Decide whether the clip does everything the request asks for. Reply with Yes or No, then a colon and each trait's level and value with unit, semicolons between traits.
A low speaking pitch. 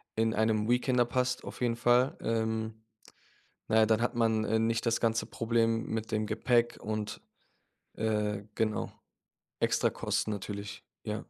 Yes: low, 110 Hz